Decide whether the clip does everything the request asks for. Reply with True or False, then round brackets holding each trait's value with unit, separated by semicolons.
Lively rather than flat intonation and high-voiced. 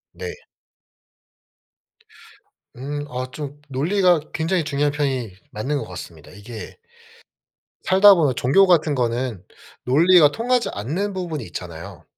False (6.0 semitones; 145 Hz)